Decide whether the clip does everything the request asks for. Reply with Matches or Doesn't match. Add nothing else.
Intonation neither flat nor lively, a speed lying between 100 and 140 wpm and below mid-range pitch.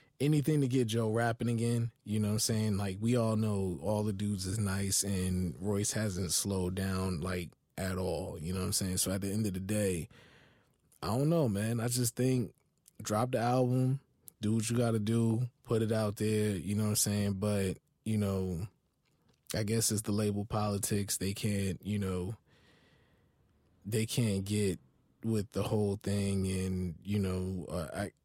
Doesn't match